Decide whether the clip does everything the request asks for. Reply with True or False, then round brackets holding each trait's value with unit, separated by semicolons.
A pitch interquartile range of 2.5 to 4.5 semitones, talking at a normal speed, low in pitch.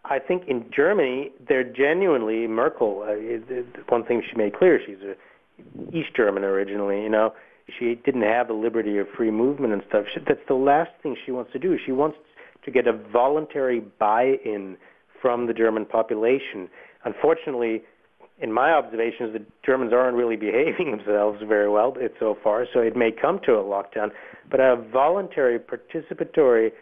True (3.4 semitones; 175 wpm; 115 Hz)